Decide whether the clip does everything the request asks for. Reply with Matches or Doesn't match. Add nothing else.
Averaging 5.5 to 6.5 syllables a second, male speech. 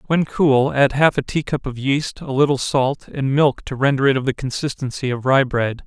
Doesn't match